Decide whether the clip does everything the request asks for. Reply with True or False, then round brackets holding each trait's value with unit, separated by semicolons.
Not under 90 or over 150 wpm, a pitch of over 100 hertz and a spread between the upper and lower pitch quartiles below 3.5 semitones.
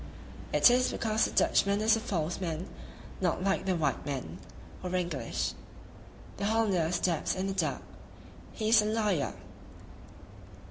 False (140 wpm; 190 Hz; 4.0 semitones)